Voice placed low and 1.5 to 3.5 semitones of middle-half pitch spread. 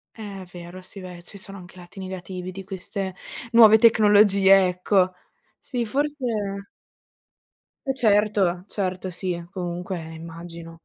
No: high, 190 Hz; narrow, 2.5 semitones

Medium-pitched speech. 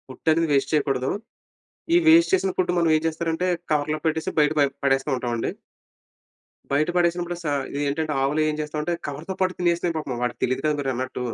Yes: medium, 155 Hz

